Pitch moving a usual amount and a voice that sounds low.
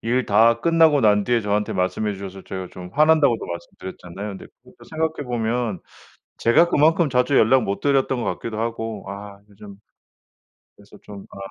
Yes: average, 4.8 semitones; low, 115 Hz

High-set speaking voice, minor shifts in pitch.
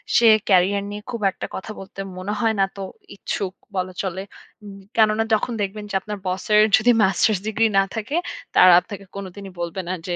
Yes: high, 200 Hz; narrow, 2.3 semitones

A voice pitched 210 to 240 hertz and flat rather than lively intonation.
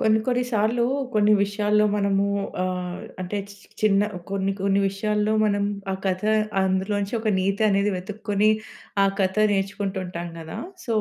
No: high, 200 Hz; narrow, 1.8 semitones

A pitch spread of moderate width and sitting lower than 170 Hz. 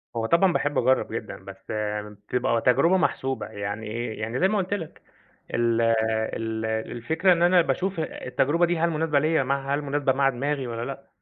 No: wide, 6.1 semitones; low, 135 Hz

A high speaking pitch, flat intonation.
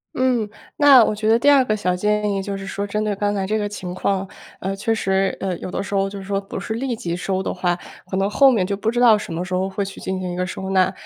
Yes: high, 200 Hz; narrow, 2.1 semitones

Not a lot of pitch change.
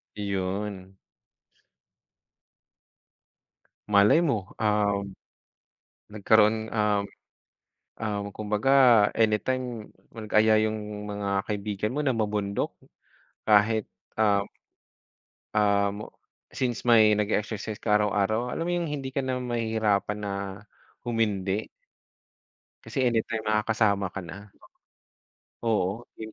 Yes: narrow, 1.7 semitones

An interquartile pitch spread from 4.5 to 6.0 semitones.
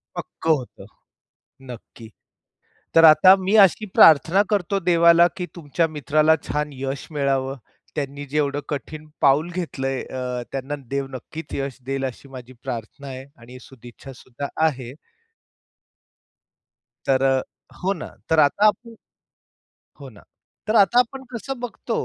No: average, 4.1 semitones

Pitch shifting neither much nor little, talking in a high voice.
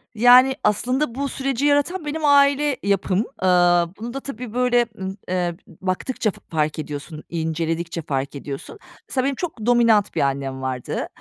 No: wide, 8.1 semitones; high, 210 Hz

